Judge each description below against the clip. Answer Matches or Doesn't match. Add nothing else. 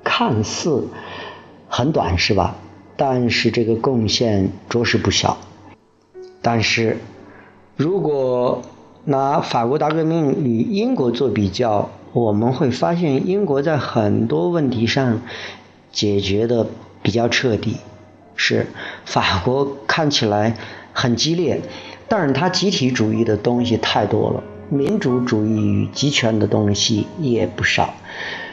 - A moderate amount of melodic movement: Matches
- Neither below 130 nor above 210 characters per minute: Matches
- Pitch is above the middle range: Doesn't match